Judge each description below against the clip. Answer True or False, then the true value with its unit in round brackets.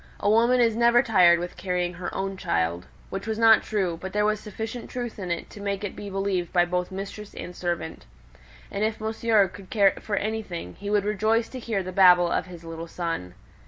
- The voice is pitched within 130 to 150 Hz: False (195 Hz)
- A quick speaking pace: True (210 wpm)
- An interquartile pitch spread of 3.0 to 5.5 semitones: True (3.4 semitones)